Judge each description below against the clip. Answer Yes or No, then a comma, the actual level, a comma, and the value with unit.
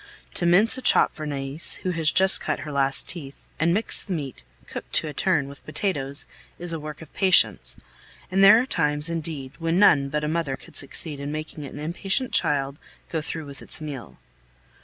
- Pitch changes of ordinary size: Yes, average, 3.4 semitones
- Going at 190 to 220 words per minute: Yes, average, 200 wpm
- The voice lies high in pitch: No, medium, 155 Hz